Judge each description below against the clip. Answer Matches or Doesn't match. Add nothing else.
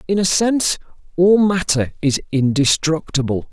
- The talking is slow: Matches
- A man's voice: Matches